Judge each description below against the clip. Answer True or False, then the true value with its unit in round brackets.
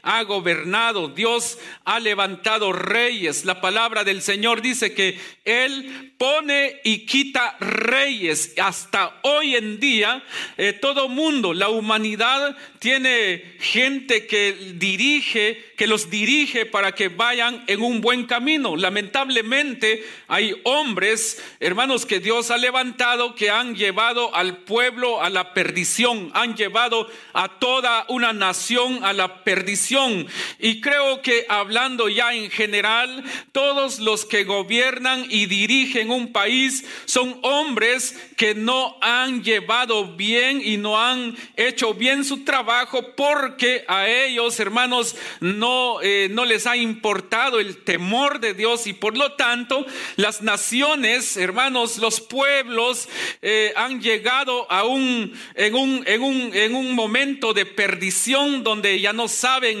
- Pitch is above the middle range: True (235 Hz)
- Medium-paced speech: True (135 wpm)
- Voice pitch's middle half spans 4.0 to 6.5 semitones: False (3.5 semitones)